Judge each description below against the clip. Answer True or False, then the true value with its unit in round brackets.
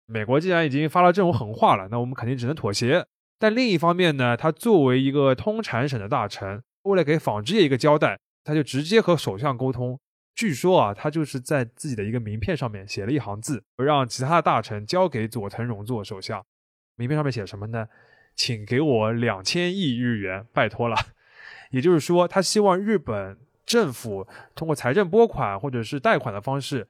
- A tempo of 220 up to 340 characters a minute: True (305 characters per minute)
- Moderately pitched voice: False (130 Hz)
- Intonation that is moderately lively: False (5.8 semitones)